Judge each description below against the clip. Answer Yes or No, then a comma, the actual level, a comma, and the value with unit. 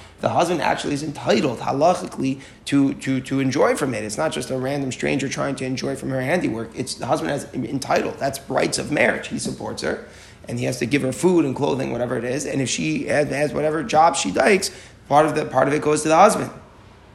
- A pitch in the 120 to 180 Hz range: Yes, low, 135 Hz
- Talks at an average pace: No, fast, 230 wpm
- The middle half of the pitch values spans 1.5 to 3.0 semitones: Yes, narrow, 2.4 semitones